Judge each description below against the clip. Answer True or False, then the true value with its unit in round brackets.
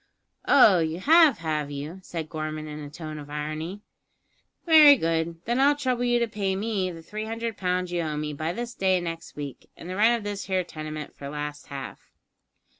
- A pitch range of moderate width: False (6.0 semitones)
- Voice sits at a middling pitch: True (175 Hz)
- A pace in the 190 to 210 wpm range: True (200 wpm)